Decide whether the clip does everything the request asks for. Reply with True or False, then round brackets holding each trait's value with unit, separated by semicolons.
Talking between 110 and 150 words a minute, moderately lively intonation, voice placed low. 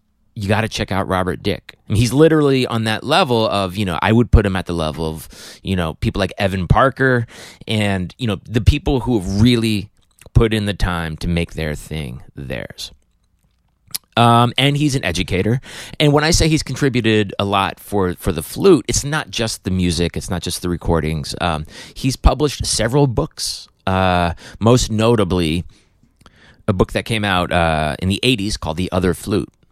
False (195 wpm; 4.9 semitones; 105 Hz)